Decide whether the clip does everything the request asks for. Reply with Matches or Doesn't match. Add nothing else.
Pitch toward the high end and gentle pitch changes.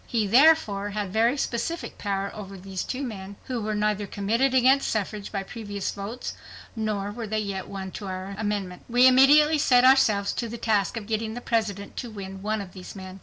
Doesn't match